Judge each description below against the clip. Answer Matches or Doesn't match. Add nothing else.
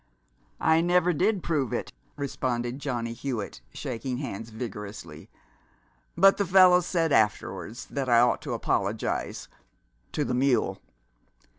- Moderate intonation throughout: Doesn't match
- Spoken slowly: Matches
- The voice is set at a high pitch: Doesn't match